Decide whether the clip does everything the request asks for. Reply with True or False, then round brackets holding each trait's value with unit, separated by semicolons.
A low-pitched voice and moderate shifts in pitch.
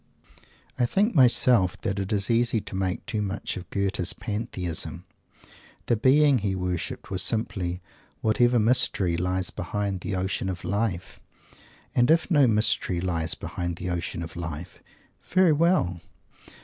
True (100 Hz; 4.7 semitones)